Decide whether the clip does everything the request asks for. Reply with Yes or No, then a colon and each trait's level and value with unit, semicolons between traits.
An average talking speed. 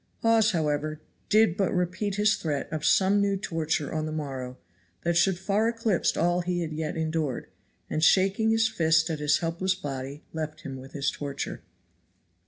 Yes: average, 175 wpm